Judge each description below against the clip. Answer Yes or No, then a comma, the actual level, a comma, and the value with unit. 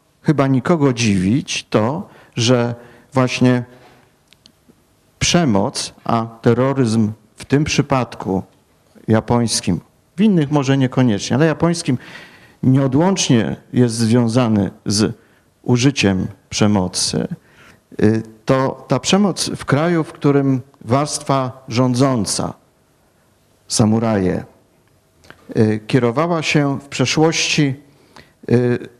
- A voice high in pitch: No, low, 125 Hz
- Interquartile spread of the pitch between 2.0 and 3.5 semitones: No, average, 4.0 semitones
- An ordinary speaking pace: No, slow, 80 wpm